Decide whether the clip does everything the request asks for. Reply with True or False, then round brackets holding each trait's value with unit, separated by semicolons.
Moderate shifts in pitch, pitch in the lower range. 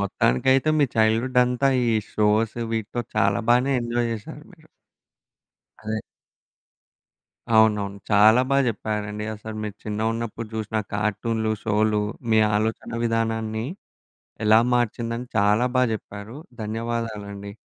False (1.7 semitones; 110 Hz)